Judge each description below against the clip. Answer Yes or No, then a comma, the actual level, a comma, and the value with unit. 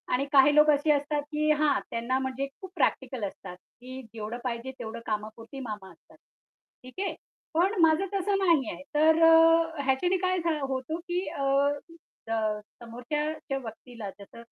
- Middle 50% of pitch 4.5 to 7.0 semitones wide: Yes, average, 5.1 semitones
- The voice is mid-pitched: No, very high, 270 Hz